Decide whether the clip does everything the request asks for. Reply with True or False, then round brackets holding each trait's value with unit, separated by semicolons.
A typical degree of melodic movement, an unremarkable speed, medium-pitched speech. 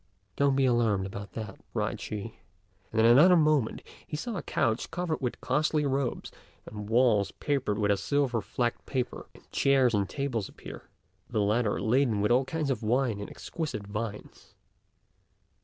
False (4.8 semitones; 165 wpm; 120 Hz)